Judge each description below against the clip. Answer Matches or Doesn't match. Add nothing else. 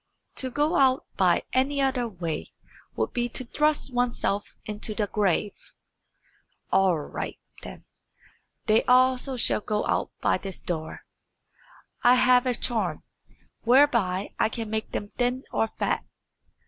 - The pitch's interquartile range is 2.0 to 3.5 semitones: Doesn't match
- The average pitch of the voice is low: Doesn't match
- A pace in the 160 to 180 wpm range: Doesn't match